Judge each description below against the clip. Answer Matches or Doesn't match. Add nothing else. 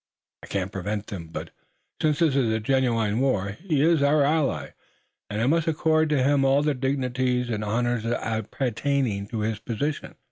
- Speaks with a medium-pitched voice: Doesn't match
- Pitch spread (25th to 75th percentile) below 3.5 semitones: Doesn't match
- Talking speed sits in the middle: Matches